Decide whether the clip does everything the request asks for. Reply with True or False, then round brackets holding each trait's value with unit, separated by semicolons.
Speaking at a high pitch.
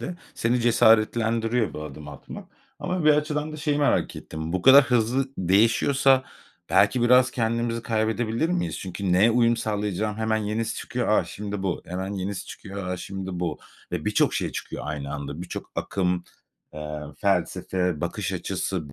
False (110 Hz)